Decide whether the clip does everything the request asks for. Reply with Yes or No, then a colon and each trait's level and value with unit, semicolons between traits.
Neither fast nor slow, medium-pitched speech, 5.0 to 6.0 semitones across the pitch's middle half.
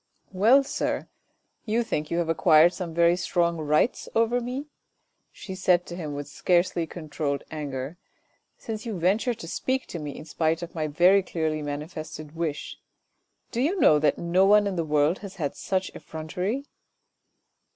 No: average, 175 wpm; medium, 170 Hz; average, 4.1 semitones